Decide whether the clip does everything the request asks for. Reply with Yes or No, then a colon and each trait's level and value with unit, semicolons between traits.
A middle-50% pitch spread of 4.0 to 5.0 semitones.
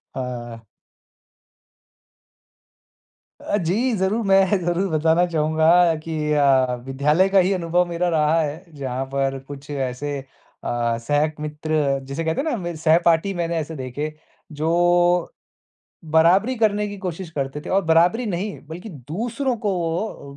Yes: average, 4.4 semitones